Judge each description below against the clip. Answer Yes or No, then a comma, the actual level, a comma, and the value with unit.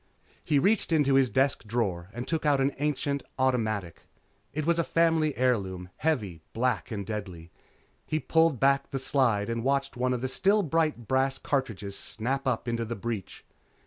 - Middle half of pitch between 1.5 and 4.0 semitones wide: No, average, 4.6 semitones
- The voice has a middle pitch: No, low, 130 Hz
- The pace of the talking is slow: No, average, 175 wpm